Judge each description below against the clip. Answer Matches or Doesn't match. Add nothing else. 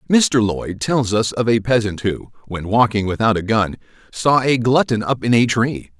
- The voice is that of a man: Matches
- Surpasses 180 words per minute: Matches